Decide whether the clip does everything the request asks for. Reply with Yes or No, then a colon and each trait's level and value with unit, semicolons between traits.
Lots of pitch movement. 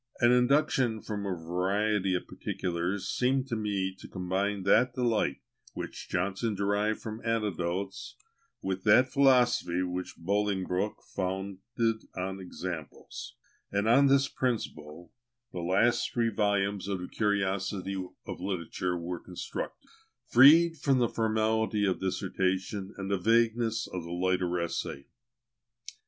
No: average, 3.6 semitones